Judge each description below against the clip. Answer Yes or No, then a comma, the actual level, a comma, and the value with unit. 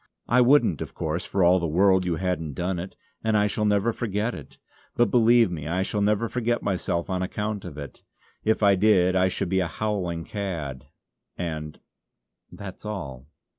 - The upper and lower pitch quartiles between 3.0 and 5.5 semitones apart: Yes, average, 3.8 semitones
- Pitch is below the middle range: Yes, very low, 95 Hz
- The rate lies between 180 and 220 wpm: Yes, average, 185 wpm